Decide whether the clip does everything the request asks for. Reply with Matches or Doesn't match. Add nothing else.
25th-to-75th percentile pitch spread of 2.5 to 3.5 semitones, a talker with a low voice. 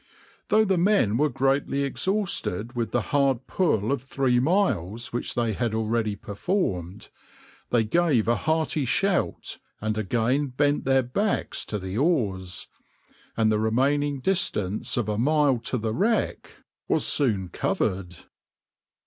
Doesn't match